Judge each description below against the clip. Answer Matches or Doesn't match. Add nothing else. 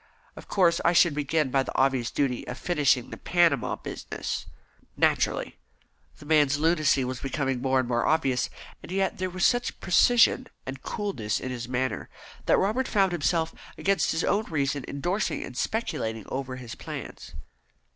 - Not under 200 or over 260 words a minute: Doesn't match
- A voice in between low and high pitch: Matches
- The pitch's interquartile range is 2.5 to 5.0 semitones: Doesn't match